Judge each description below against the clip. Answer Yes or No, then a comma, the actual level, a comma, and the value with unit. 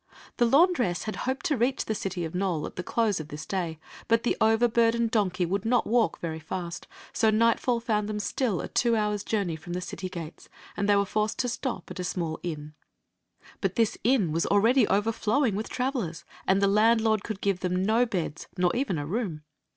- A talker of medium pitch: No, high, 210 Hz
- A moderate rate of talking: No, fast, 210 wpm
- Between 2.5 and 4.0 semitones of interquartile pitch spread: No, average, 4.4 semitones